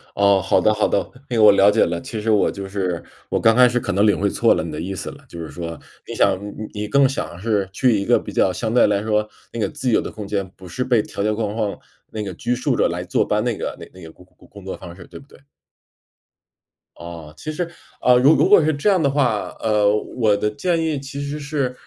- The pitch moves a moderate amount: Yes, average, 4.6 semitones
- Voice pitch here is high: No, low, 105 Hz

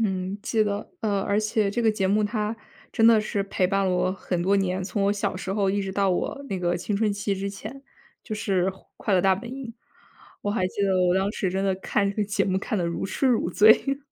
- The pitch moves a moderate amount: No, narrow, 2.0 semitones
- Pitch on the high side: Yes, high, 200 Hz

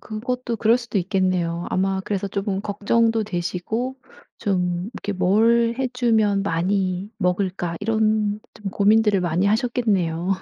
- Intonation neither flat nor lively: Yes, average, 3.3 semitones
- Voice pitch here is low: No, high, 205 Hz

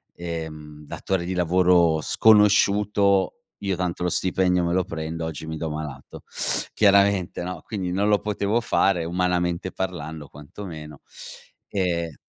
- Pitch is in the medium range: No, very low, 90 Hz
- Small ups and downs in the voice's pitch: No, average, 3.2 semitones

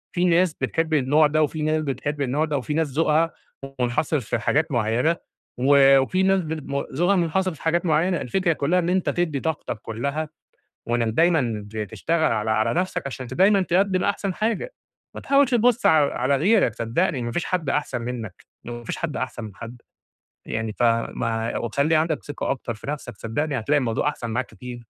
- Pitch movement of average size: No, wide, 5.7 semitones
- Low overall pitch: No, medium, 150 Hz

